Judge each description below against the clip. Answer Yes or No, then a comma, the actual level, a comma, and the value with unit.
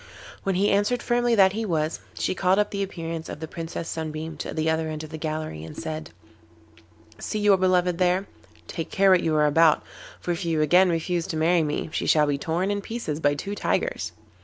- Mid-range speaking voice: Yes, medium, 165 Hz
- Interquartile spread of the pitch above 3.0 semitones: Yes, average, 3.5 semitones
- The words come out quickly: Yes, fast, 220 wpm